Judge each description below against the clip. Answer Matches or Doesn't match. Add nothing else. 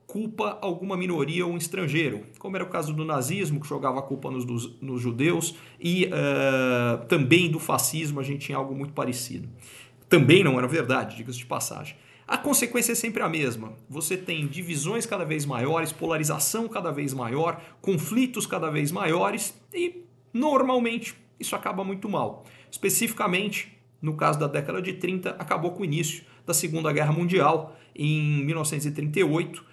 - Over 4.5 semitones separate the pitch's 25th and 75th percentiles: Matches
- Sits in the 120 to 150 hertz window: Doesn't match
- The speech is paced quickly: Doesn't match